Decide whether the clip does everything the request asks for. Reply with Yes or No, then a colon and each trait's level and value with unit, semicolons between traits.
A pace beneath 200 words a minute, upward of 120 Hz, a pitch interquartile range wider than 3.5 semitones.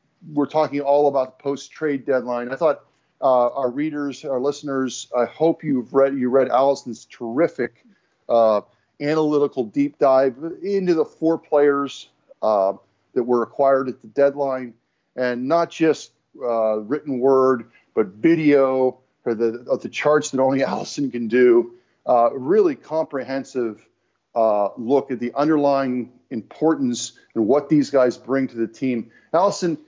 No: average, 150 wpm; low, 135 Hz; average, 3.2 semitones